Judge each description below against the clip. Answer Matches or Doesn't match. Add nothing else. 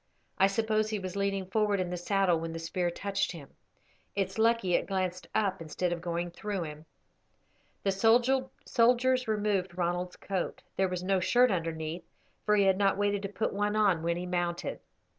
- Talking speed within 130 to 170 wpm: Doesn't match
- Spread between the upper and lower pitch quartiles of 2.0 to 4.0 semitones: Matches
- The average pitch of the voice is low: Doesn't match